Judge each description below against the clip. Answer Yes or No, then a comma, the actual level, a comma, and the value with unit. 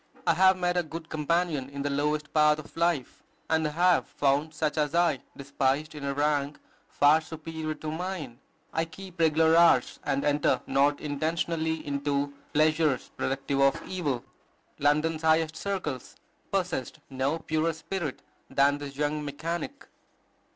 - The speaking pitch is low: No, medium, 155 Hz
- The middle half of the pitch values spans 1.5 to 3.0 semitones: Yes, narrow, 2.4 semitones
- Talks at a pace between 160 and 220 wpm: No, average, 150 wpm